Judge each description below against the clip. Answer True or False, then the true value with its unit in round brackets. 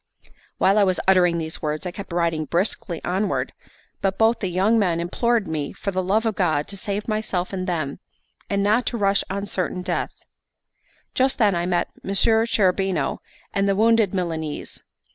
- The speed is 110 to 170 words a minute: False (180 wpm)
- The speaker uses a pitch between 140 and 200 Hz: True (190 Hz)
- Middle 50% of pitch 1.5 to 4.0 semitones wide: True (3.1 semitones)